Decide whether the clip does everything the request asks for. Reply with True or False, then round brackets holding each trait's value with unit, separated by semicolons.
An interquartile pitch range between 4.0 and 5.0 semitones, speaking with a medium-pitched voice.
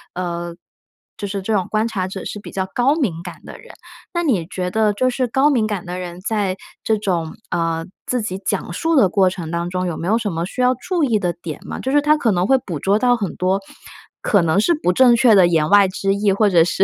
False (4.6 semitones; 195 Hz)